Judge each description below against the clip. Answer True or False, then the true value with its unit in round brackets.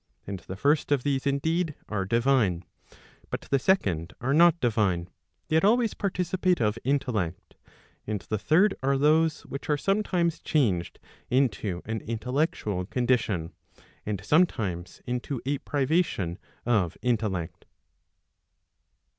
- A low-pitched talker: True (125 Hz)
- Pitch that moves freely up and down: True (7.7 semitones)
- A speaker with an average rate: False (120 wpm)